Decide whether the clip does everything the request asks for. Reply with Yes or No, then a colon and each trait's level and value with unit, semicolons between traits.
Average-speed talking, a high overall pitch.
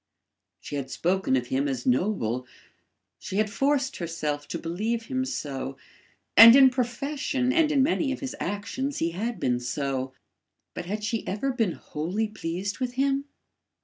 Yes: average, 160 wpm; high, 210 Hz